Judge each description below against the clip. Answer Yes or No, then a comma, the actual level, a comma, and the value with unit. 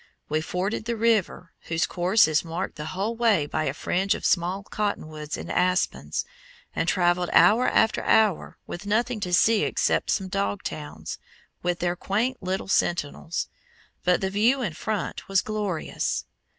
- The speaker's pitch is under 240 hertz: Yes, high, 190 Hz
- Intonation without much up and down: No, average, 3.6 semitones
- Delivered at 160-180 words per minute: Yes, average, 165 wpm